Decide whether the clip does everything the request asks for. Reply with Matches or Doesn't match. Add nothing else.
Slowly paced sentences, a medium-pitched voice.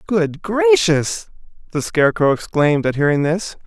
Matches